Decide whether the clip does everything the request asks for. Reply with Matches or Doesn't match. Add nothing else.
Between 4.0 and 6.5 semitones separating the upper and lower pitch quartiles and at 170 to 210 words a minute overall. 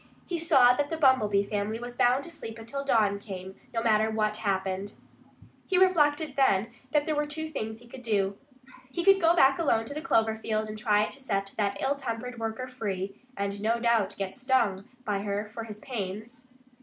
Matches